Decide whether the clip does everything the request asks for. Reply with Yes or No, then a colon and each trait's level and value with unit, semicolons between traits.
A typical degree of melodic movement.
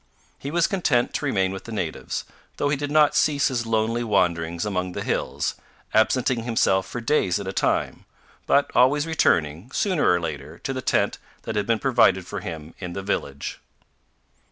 No: wide, 6.8 semitones